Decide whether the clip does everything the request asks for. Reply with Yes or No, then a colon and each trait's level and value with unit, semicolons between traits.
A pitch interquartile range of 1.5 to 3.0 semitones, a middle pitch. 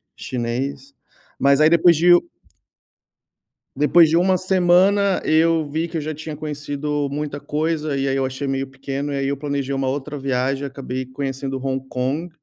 Yes: average, 2.7 semitones; medium, 145 Hz